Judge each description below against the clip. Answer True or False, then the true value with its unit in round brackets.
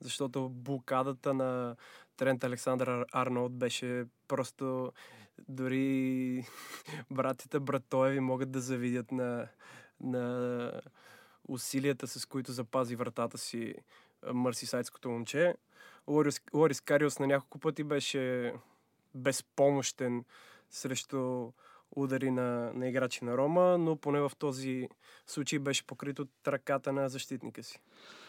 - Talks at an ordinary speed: False (110 wpm)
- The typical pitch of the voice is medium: False (130 Hz)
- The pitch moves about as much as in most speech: False (1.9 semitones)